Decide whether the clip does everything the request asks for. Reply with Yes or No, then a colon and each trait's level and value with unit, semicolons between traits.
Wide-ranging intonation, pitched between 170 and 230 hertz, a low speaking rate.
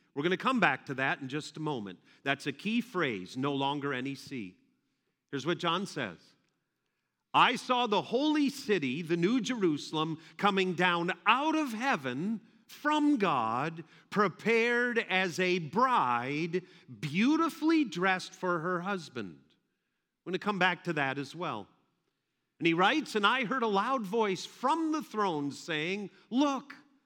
No: wide, 7.4 semitones; medium, 185 Hz; average, 155 wpm